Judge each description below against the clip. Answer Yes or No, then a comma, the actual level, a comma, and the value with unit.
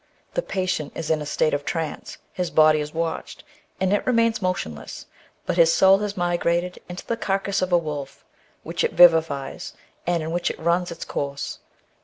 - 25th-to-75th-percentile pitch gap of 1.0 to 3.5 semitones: Yes, average, 3.1 semitones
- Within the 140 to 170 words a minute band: No, average, 185 wpm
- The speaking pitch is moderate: Yes, medium, 170 Hz